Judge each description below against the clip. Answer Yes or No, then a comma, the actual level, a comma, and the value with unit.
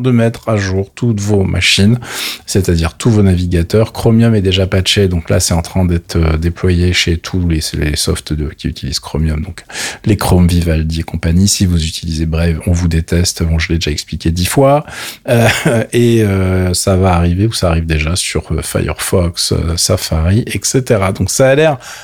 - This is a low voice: Yes, very low, 90 Hz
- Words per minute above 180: Yes, average, 190 wpm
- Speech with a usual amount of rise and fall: Yes, average, 3.7 semitones